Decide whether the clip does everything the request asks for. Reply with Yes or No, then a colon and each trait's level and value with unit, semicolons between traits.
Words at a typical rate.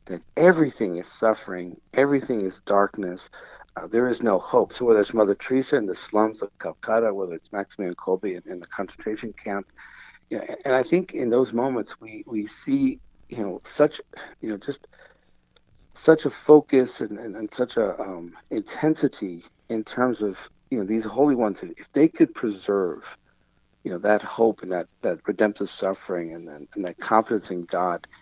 Yes: average, 180 wpm